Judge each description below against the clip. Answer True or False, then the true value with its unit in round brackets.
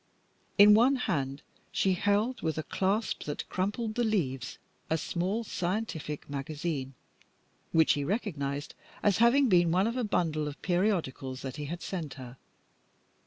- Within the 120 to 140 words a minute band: False (150 wpm)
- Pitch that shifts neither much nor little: False (6.3 semitones)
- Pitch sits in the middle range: True (175 Hz)